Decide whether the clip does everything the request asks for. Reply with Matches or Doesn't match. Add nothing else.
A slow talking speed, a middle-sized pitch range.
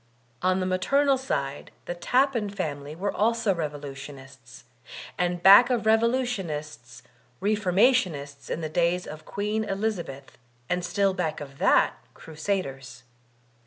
Doesn't match